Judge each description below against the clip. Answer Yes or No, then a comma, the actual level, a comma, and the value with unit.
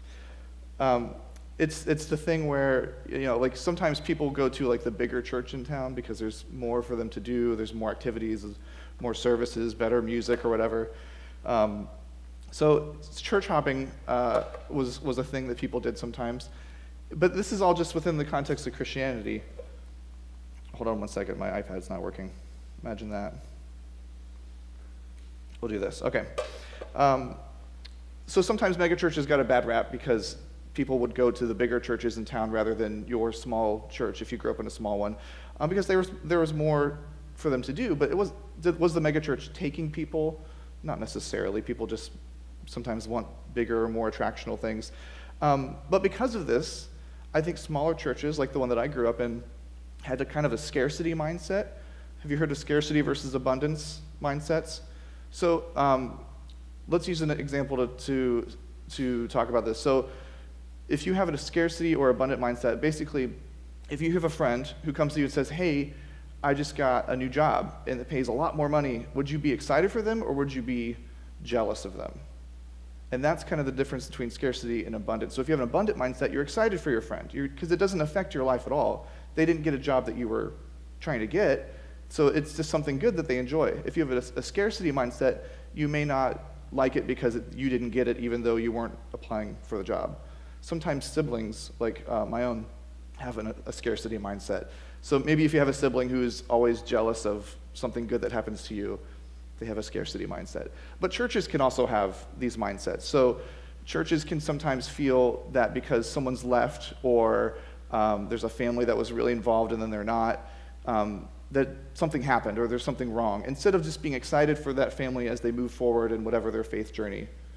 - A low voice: Yes, low, 120 Hz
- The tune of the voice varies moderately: No, wide, 8.6 semitones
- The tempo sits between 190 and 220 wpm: Yes, average, 200 wpm